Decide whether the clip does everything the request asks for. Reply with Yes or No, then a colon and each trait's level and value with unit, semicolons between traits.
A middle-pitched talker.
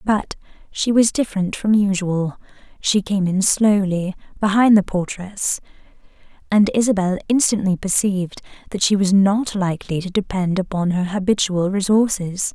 No: high, 195 Hz